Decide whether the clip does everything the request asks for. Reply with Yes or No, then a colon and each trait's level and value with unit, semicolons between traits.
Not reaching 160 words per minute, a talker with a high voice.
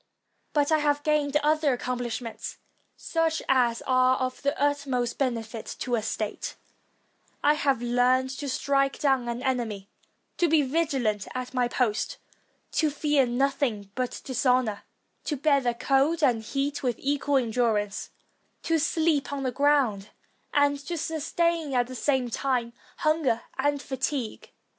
Yes: average, 145 wpm; very high, 265 Hz